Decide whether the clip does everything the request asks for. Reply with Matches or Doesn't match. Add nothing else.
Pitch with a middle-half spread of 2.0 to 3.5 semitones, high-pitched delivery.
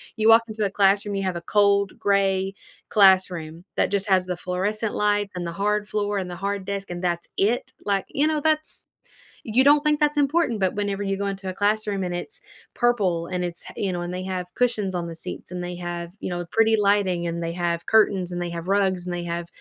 Matches